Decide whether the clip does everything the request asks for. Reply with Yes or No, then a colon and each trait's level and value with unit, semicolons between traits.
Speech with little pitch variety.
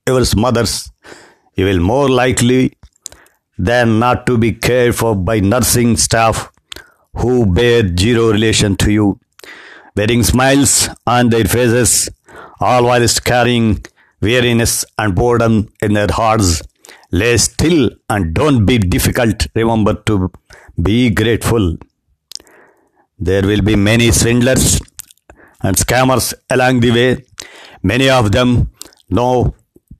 No: average, 3.3 semitones